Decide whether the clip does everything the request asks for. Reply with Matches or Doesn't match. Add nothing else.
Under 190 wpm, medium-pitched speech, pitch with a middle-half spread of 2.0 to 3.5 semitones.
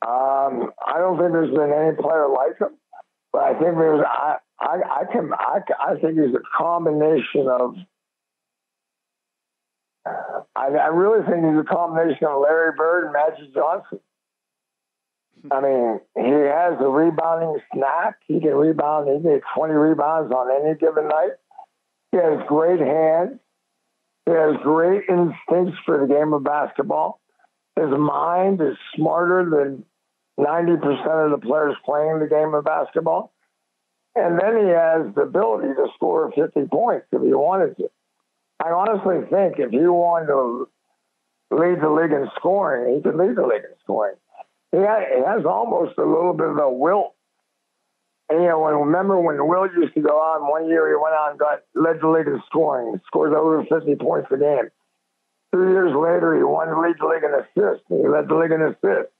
Matches